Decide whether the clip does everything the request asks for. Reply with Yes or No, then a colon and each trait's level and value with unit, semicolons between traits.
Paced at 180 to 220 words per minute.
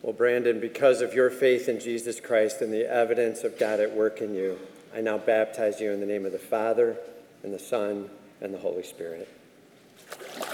Yes: average, 200 wpm